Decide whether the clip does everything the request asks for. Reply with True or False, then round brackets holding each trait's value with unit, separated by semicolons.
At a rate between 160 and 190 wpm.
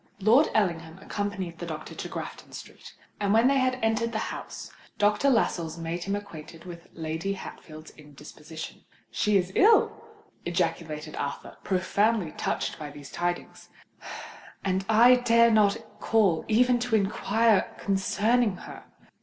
False (135 wpm)